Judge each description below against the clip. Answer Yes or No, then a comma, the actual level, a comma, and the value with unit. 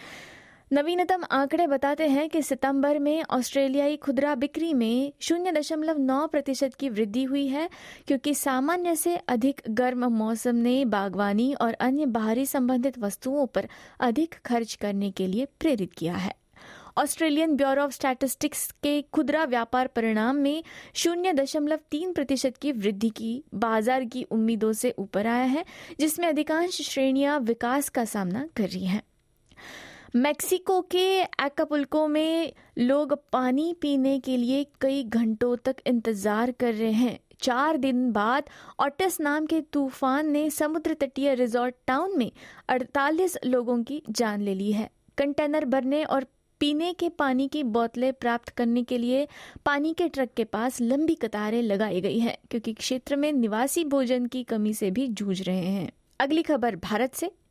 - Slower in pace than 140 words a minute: No, average, 155 wpm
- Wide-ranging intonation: No, average, 3.9 semitones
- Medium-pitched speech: No, very high, 270 Hz